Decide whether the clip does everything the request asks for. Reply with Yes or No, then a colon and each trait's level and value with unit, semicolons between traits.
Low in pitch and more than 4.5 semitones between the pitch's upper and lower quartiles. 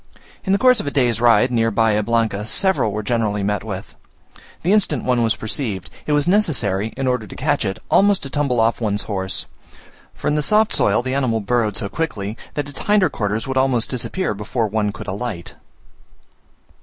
Yes: low, 115 Hz; average, 5.3 semitones